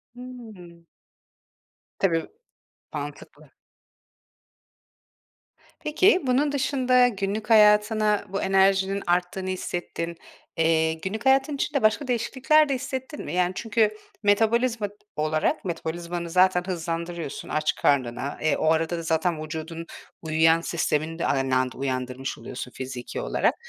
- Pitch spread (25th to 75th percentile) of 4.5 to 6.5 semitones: Yes, wide, 5.6 semitones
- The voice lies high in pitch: No, medium, 180 Hz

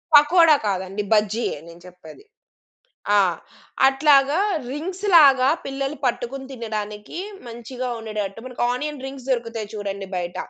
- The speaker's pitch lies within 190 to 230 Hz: No, high, 240 Hz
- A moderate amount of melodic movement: Yes, average, 4.8 semitones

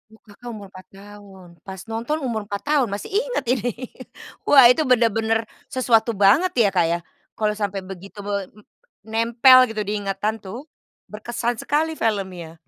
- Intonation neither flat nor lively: Yes, average, 3.5 semitones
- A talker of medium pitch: No, high, 220 Hz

